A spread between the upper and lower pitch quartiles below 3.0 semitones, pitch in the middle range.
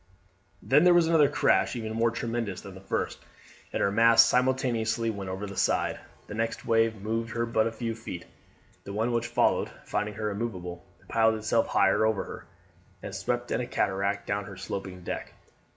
No: narrow, 2.6 semitones; low, 110 Hz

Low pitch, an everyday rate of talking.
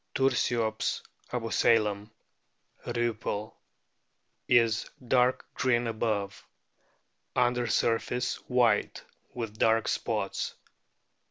No: low, 115 Hz; slow, 70 wpm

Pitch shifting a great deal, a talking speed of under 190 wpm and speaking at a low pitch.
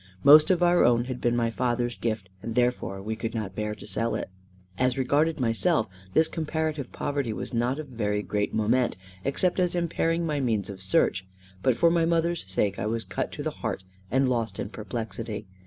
No: wide, 5.7 semitones; average, 200 wpm; low, 120 Hz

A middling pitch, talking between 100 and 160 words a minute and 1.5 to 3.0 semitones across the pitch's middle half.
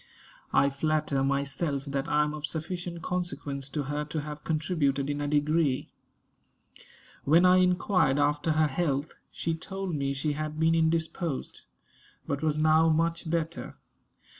Yes: medium, 155 Hz; average, 145 wpm; narrow, 2.5 semitones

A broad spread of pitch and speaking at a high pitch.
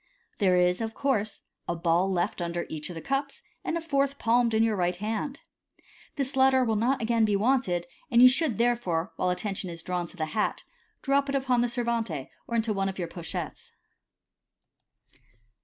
Yes: wide, 6.0 semitones; high, 220 Hz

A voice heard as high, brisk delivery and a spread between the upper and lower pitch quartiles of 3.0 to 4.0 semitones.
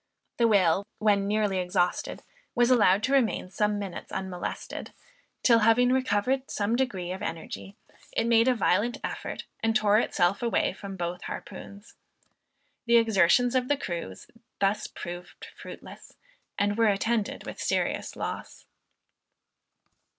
No: high, 210 Hz; slow, 135 wpm; average, 3.6 semitones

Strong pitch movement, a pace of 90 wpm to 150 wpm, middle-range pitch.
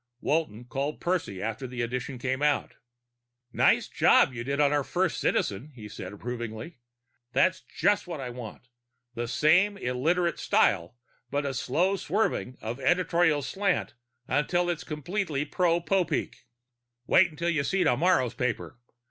Yes: wide, 6.0 semitones; average, 140 wpm; medium, 145 Hz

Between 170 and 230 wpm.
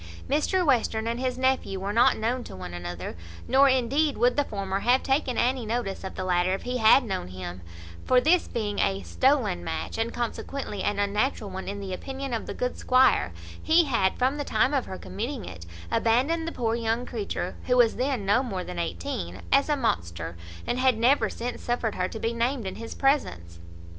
Yes: fast, 205 wpm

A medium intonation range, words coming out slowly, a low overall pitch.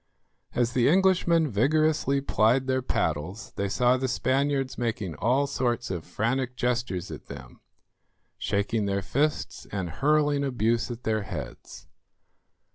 Yes: average, 4.7 semitones; slow, 130 wpm; low, 125 Hz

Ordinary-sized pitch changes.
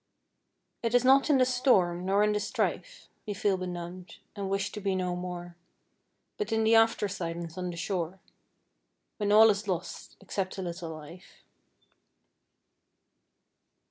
Yes: average, 3.2 semitones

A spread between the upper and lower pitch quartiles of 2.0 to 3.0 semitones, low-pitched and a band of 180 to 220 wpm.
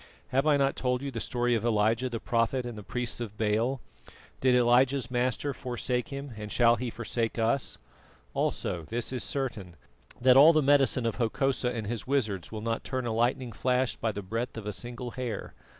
Yes: narrow, 2.4 semitones; low, 120 Hz; average, 200 wpm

